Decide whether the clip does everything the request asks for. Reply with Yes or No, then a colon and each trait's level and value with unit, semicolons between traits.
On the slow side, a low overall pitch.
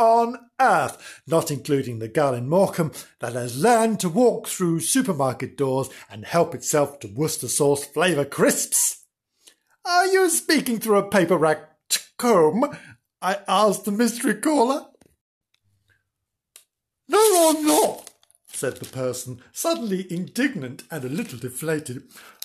No: slow, 130 wpm; medium, 175 Hz